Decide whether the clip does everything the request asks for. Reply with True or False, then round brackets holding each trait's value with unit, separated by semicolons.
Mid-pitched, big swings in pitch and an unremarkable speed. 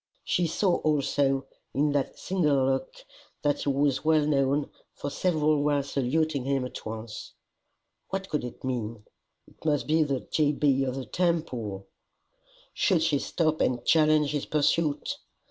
False (145 Hz; 2.7 semitones; 150 wpm)